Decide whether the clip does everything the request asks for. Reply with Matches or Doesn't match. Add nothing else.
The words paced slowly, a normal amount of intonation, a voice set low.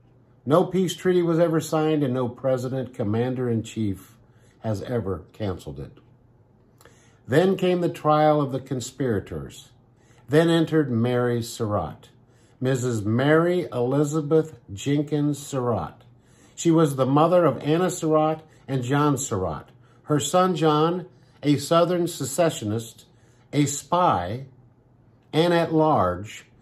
Matches